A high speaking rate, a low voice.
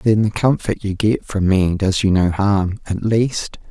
Yes: fast, 210 wpm; low, 100 Hz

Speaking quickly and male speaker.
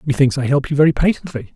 Yes: fast, 230 wpm; male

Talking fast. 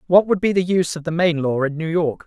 Yes: fast, 320 wpm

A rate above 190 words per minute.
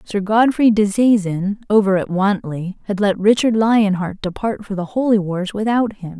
No: average, 175 wpm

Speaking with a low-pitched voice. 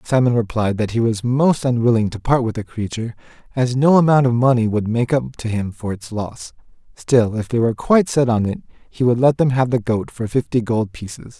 Yes: low, 120 Hz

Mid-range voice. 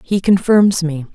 Yes: medium, 180 Hz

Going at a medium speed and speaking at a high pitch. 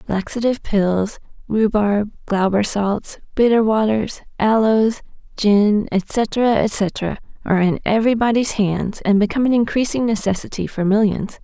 No: slow, 120 wpm; high, 215 Hz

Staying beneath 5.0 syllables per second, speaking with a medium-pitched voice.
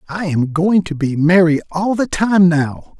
Yes: 4.1 syllables/s; medium, 170 Hz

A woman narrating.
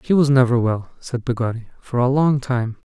No: male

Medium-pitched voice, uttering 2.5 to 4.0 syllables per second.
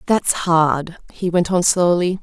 Yes: medium, 175 Hz; 3.6 syllables/s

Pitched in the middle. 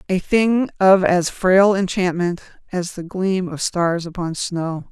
Yes: medium, 180 Hz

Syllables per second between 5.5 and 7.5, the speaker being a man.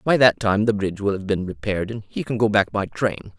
Yes: 6.2 syllables/s; male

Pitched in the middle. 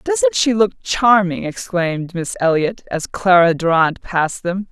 Yes: medium, 175 Hz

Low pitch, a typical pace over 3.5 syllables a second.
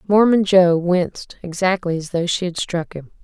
No: medium, 180 Hz; 4.8 syllables/s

